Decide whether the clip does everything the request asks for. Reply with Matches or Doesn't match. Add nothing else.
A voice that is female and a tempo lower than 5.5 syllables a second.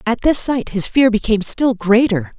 Matches